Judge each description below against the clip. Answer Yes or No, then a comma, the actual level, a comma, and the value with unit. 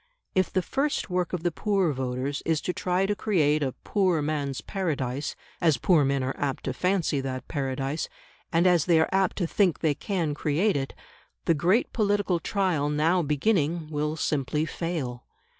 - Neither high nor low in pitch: Yes, medium, 160 Hz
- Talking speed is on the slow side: No, average, 175 wpm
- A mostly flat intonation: No, average, 4.4 semitones